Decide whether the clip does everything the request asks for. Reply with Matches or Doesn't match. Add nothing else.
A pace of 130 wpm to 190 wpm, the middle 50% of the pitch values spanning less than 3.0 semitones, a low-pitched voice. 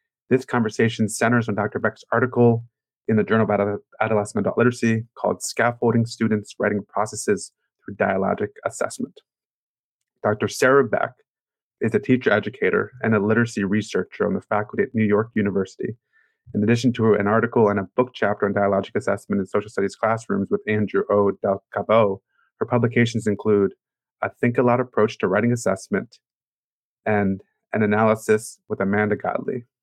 Matches